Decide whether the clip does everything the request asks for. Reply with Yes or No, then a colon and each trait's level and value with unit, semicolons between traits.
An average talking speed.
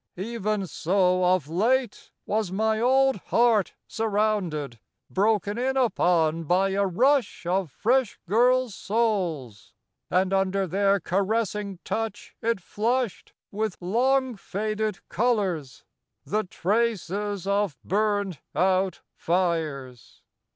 No: slow, 105 wpm